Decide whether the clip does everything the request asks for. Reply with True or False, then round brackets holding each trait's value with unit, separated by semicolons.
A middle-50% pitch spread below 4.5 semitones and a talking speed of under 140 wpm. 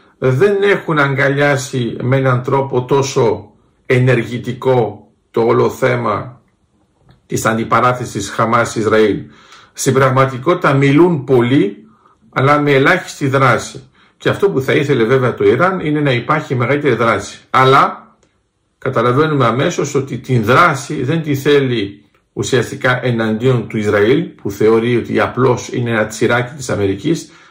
True (3.2 semitones; 125 wpm)